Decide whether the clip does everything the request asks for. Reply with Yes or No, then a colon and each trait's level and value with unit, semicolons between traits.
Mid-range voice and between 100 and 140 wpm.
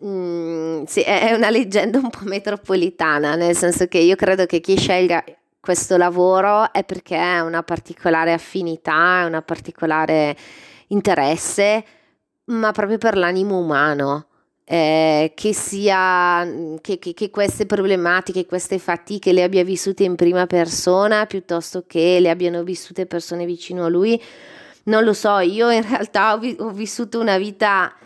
No: medium, 180 Hz; average, 150 wpm